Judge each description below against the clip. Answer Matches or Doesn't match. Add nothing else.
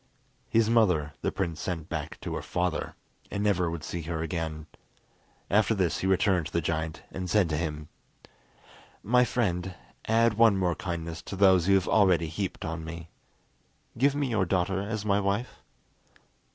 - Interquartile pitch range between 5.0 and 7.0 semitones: Doesn't match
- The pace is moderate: Matches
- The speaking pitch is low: Matches